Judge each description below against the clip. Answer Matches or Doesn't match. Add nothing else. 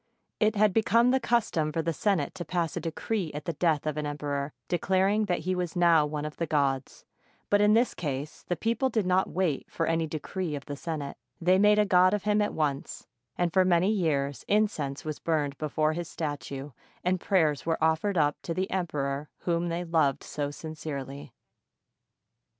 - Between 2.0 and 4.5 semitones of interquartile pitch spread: Matches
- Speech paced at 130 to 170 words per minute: Doesn't match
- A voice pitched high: Doesn't match